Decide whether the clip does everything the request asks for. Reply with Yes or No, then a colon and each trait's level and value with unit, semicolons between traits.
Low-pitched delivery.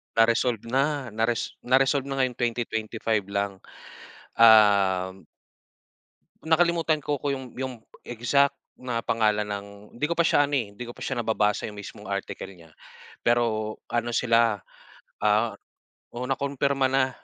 Yes: low, 120 Hz